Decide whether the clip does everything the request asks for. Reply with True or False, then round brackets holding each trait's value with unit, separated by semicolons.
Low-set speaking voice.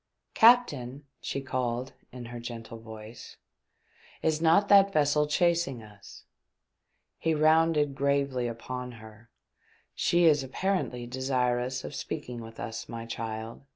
True (130 Hz)